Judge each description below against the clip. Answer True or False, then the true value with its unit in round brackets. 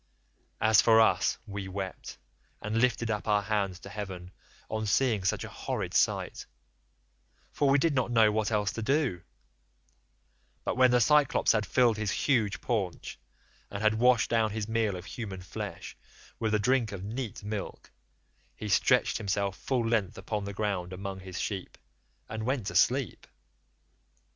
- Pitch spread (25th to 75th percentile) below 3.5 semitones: True (2.8 semitones)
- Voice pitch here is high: False (110 Hz)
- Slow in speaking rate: False (165 wpm)